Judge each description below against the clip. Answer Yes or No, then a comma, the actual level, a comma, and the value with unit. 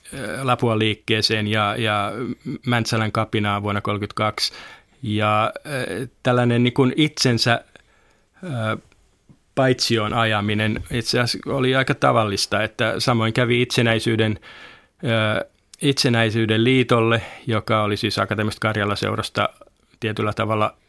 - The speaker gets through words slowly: Yes, slow, 90 wpm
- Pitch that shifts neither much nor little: No, narrow, 2.3 semitones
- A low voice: Yes, low, 110 Hz